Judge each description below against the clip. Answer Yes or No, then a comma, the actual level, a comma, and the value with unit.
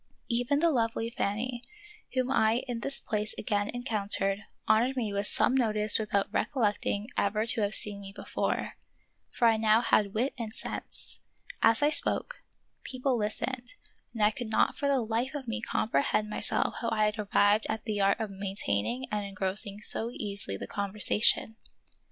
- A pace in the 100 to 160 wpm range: No, average, 175 wpm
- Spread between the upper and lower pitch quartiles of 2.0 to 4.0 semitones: Yes, average, 2.9 semitones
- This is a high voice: Yes, high, 220 Hz